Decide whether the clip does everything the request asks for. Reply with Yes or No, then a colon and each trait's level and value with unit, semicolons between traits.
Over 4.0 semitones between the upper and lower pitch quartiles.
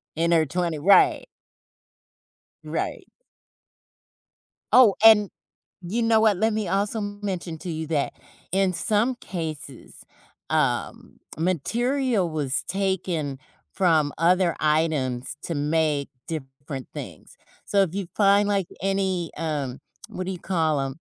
Yes: average, 4.4 semitones